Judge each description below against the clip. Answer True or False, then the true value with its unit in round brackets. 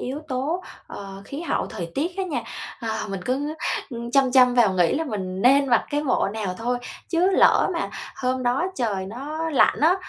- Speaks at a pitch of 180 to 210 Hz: False (255 Hz)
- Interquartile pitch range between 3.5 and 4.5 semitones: False (5.0 semitones)